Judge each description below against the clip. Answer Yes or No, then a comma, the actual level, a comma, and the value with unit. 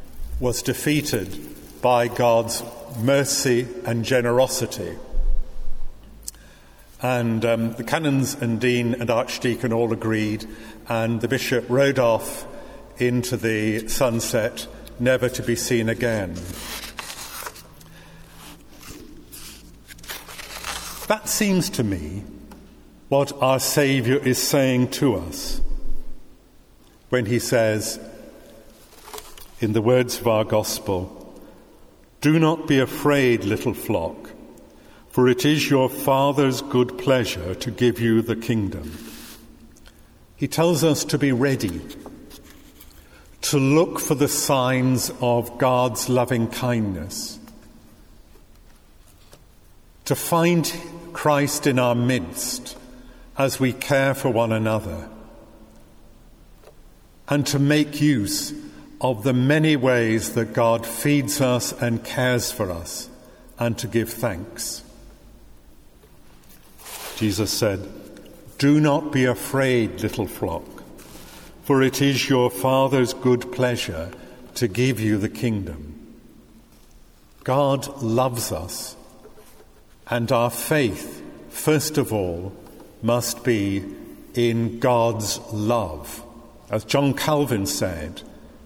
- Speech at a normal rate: No, slow, 105 wpm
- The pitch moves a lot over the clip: No, average, 3.3 semitones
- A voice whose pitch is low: Yes, low, 120 Hz